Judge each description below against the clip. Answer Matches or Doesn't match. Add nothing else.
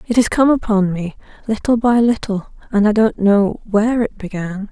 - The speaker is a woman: Matches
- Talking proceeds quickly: Doesn't match